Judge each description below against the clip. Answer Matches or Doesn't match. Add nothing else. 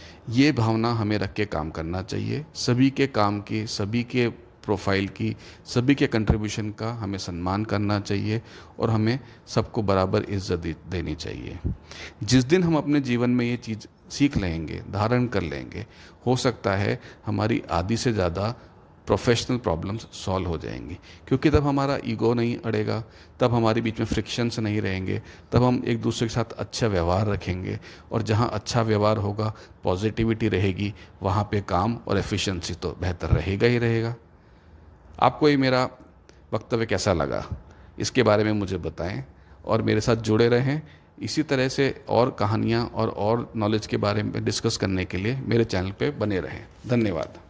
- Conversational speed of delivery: Matches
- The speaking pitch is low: Matches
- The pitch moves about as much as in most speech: Matches